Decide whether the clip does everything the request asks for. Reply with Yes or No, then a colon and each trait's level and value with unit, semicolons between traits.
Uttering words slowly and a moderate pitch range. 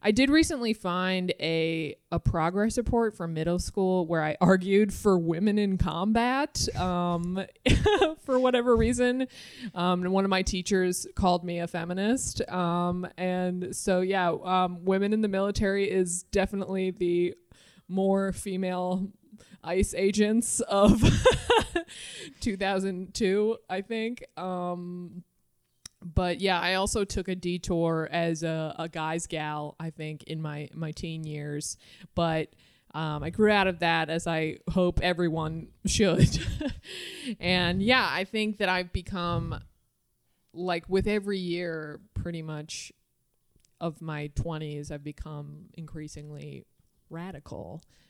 Yes: slow, 130 wpm; average, 3.2 semitones